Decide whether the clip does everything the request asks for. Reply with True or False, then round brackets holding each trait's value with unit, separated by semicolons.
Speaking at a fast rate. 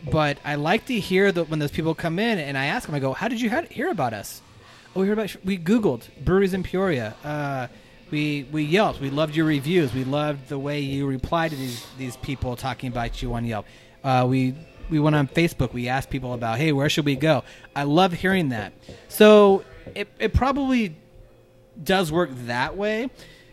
True (210 wpm)